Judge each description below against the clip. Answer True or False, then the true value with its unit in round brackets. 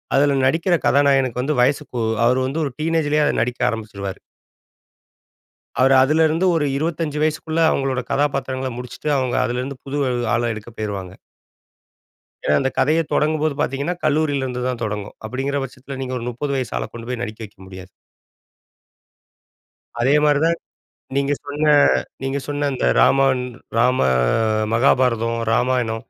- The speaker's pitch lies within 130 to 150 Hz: True (135 Hz)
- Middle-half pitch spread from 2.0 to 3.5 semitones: True (3.2 semitones)